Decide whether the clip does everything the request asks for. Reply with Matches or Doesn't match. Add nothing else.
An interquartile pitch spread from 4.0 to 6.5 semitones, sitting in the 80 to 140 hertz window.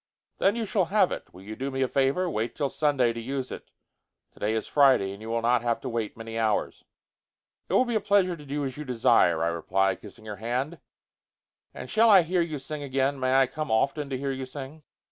Matches